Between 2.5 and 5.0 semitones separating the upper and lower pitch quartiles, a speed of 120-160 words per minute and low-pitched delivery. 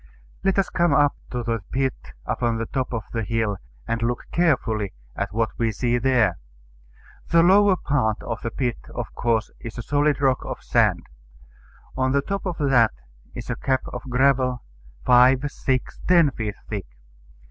No: average, 3.7 semitones; average, 170 wpm; low, 125 Hz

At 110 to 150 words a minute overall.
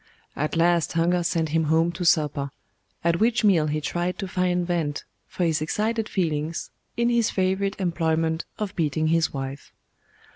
No: average, 160 wpm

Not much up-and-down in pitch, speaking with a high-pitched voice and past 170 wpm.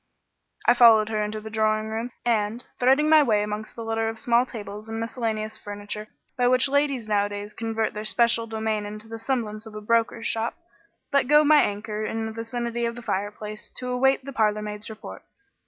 Yes: narrow, 2.0 semitones; high, 225 Hz; average, 190 wpm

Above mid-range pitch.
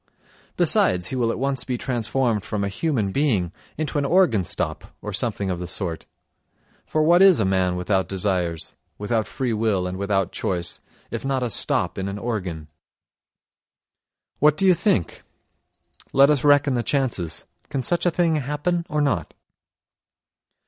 No: low, 115 Hz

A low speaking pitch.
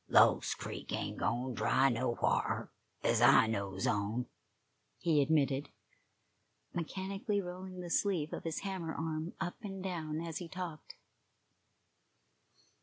No: medium, 160 Hz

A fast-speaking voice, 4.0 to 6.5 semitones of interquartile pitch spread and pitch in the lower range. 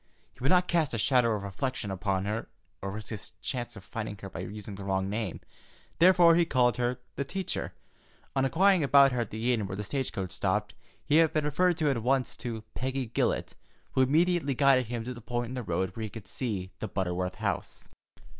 Yes: fast, 215 wpm; average, 5.2 semitones; low, 120 Hz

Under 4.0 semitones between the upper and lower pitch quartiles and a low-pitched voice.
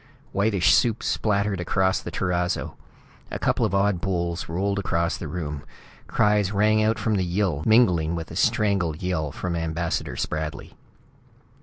Yes: average, 3.4 semitones; very low, 90 Hz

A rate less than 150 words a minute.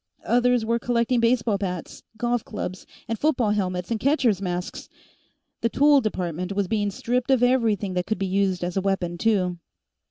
No: average, 170 wpm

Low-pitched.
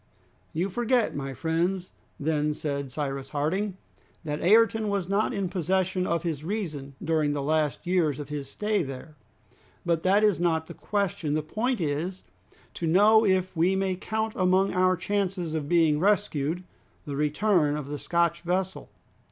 No: medium, 175 Hz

